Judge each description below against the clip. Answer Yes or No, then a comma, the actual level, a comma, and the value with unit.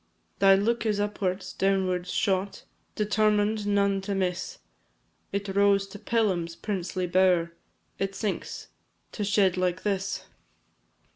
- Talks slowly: Yes, slow, 120 wpm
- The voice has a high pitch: Yes, high, 195 Hz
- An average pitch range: No, narrow, 1.8 semitones